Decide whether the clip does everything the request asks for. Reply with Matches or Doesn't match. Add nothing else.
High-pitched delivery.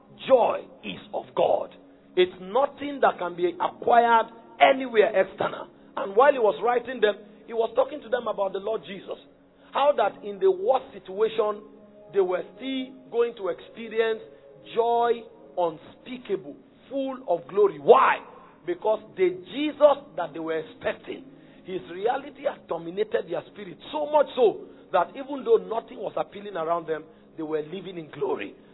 Matches